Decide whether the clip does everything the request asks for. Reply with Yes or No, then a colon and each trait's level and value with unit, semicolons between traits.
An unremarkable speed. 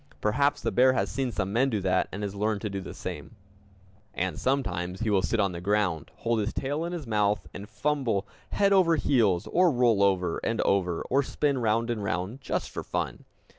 No: fast, 210 wpm